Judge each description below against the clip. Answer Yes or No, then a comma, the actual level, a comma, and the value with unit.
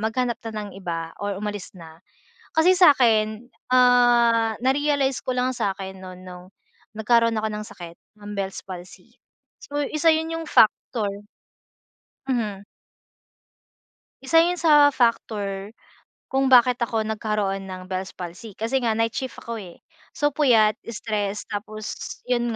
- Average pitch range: Yes, average, 4.2 semitones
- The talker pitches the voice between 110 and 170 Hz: No, high, 220 Hz